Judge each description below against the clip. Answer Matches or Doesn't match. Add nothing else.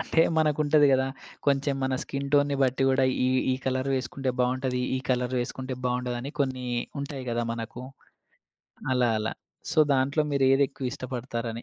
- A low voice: Matches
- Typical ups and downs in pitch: Doesn't match